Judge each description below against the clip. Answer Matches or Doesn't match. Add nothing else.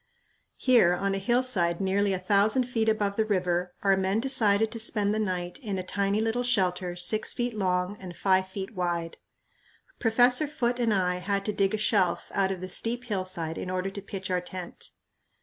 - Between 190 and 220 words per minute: Matches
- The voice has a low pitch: Doesn't match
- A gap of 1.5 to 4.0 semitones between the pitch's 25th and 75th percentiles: Matches